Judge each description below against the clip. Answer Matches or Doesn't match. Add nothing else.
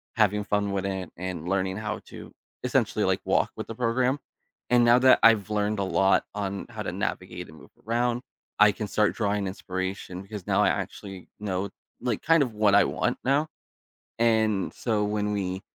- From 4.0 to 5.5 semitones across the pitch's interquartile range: Doesn't match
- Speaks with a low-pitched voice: Matches